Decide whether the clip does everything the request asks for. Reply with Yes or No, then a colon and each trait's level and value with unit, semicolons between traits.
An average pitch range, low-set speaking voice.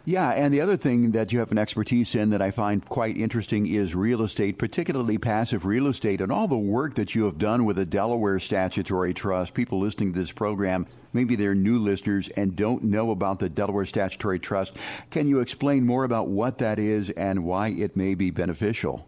Yes: average, 3.3 semitones; low, 105 Hz